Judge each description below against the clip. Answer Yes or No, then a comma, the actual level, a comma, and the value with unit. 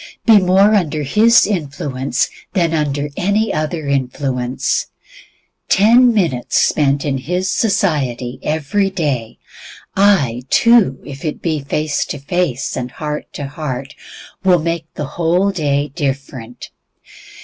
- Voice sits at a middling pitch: Yes, medium, 150 Hz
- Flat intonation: No, average, 5.3 semitones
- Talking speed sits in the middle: No, slow, 125 wpm